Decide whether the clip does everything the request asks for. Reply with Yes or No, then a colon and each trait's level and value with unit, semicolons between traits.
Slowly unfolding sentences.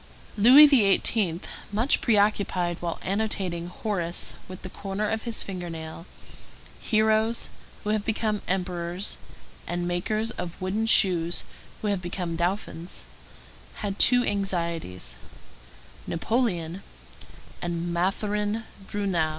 Yes: slow, 105 wpm